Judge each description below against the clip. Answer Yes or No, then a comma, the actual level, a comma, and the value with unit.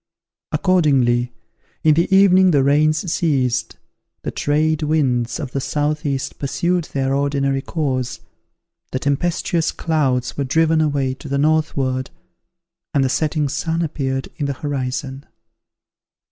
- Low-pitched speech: No, medium, 145 Hz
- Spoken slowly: Yes, slow, 125 wpm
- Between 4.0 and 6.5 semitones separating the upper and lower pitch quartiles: No, average, 2.9 semitones